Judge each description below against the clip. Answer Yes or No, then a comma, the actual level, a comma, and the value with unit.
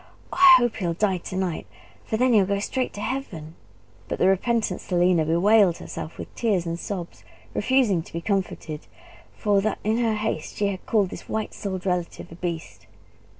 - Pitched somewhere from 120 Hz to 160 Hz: No, high, 195 Hz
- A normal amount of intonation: Yes, average, 4.1 semitones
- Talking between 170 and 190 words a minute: Yes, average, 185 wpm